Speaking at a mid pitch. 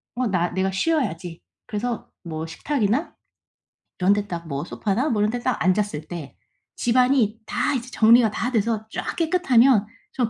No: high, 215 Hz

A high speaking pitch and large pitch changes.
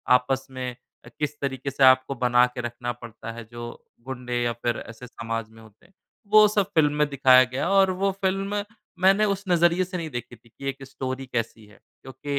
No: low, 130 Hz; wide, 5.8 semitones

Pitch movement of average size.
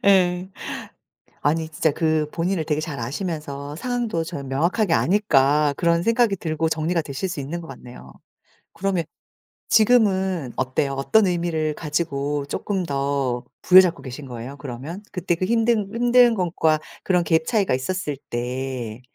Yes: average, 5.0 semitones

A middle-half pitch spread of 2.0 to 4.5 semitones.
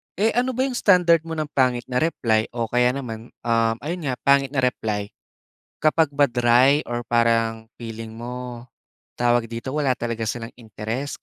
Yes: average, 3.8 semitones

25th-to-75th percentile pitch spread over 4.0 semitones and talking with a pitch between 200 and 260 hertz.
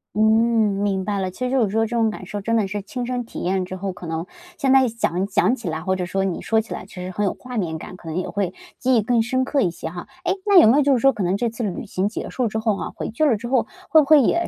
Yes: average, 4.6 semitones; high, 220 Hz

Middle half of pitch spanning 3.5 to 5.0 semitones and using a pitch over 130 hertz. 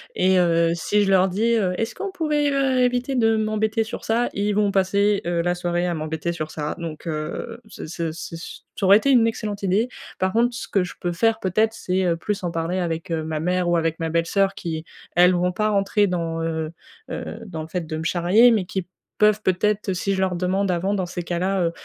Yes: average, 3.9 semitones; medium, 185 Hz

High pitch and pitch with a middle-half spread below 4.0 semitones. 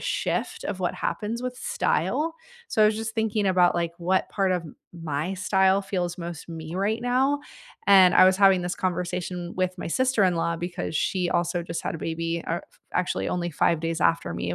No: medium, 180 Hz; average, 2.9 semitones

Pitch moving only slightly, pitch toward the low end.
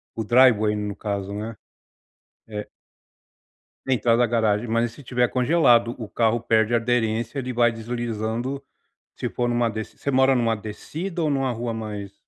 Yes: narrow, 2.0 semitones; low, 115 Hz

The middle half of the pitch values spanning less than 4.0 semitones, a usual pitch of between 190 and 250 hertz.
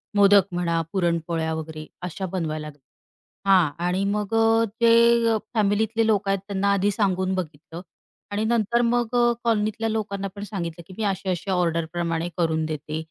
No: average, 4.4 semitones; high, 195 Hz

